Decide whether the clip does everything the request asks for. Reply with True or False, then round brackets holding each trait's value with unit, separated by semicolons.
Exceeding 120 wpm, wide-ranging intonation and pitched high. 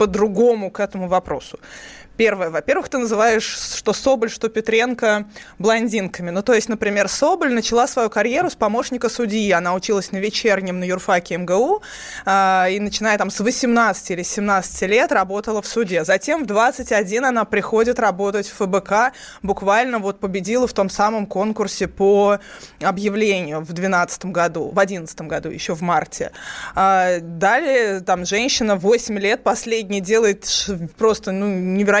False (145 wpm; 2.8 semitones; 205 Hz)